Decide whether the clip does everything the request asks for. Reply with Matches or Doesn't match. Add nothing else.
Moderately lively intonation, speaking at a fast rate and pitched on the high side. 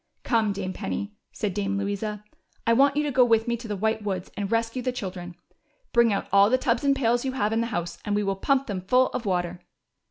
Matches